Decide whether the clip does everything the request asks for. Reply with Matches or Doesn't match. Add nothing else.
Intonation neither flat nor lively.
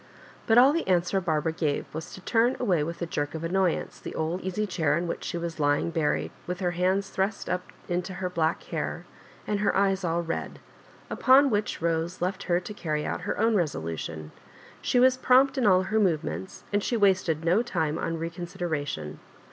Matches